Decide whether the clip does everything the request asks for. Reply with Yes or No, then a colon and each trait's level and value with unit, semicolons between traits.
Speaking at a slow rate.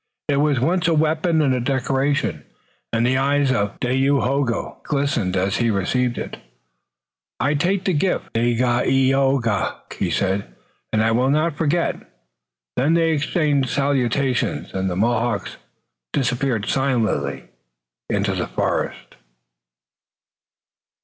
Yes: slow, 125 wpm